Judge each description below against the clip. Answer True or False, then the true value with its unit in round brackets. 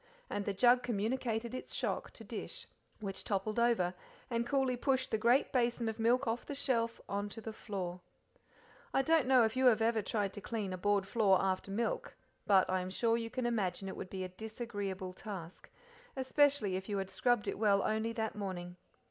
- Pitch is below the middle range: False (220 Hz)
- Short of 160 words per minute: False (200 wpm)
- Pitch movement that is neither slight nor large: True (3.5 semitones)